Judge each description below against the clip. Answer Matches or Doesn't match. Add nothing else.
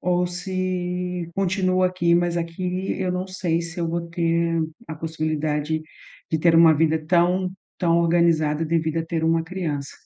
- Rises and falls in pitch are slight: Matches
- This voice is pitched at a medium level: Matches